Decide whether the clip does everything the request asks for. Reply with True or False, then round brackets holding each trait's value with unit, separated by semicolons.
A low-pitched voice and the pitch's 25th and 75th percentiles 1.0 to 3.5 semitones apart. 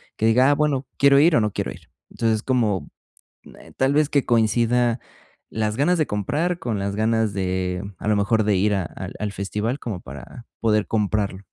False (110 Hz; 4.1 semitones)